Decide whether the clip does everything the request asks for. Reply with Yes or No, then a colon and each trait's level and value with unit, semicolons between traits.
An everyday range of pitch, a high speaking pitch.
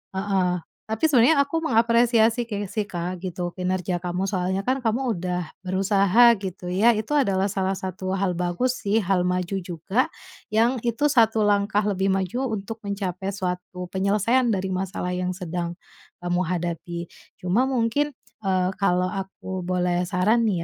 Yes: average, 3.7 semitones; high, 195 Hz